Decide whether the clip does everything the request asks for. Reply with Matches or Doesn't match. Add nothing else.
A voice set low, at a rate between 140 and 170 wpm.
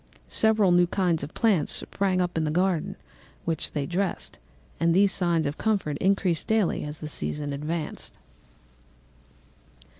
Doesn't match